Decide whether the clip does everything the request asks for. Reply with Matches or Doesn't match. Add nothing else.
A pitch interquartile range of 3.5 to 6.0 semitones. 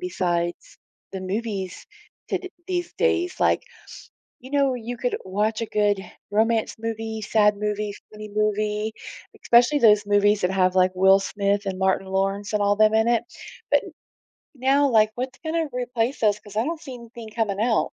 Doesn't match